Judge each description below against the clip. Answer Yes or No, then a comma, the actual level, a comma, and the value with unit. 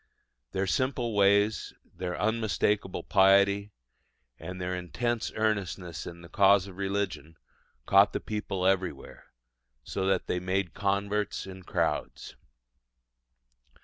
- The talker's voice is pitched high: No, very low, 95 Hz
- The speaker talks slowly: Yes, slow, 115 wpm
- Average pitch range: No, narrow, 1.9 semitones